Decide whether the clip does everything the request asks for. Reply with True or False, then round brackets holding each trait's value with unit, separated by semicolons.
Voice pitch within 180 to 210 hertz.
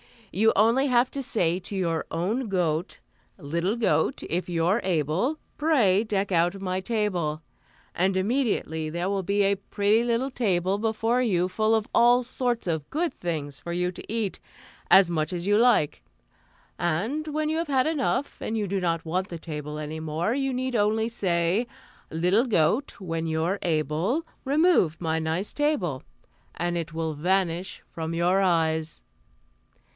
True (190 Hz)